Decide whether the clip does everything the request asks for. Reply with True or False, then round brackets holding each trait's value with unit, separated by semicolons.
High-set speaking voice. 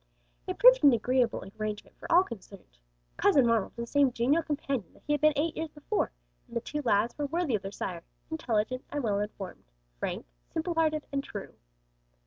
True (260 Hz)